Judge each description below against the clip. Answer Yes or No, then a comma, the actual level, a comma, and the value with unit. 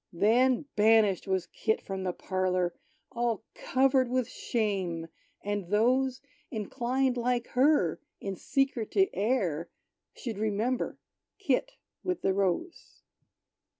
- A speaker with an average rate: No, slow, 115 wpm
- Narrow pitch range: No, average, 5.0 semitones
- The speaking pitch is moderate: No, high, 220 Hz